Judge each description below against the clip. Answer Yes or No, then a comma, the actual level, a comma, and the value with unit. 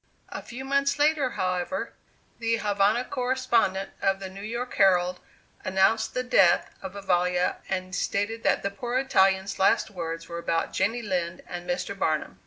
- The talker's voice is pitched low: No, high, 195 Hz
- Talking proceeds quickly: No, average, 160 wpm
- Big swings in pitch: No, average, 4.7 semitones